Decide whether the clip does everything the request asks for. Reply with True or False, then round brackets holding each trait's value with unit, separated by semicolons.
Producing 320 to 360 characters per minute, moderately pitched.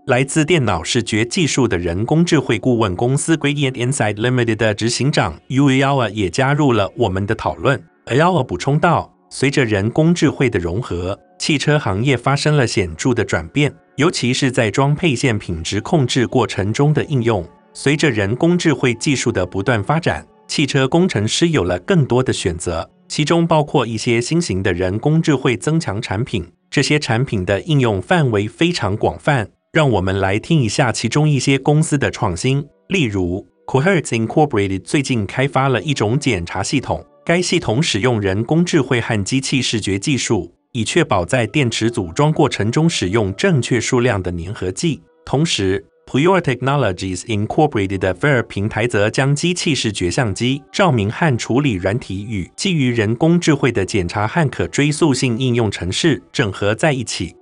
False (330 characters per minute; 125 Hz)